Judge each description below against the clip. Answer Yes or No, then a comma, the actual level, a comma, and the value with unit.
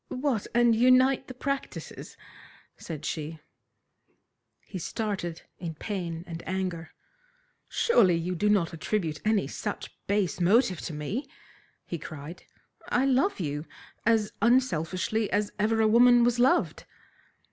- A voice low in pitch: No, high, 205 Hz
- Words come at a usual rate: No, slow, 125 wpm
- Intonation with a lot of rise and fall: Yes, wide, 6.1 semitones